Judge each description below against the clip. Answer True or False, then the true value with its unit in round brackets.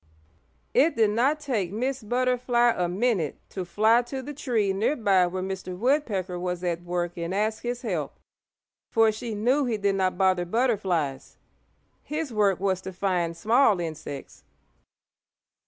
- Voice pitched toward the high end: True (205 Hz)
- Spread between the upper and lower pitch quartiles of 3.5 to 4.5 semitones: False (5.1 semitones)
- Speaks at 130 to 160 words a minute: True (155 wpm)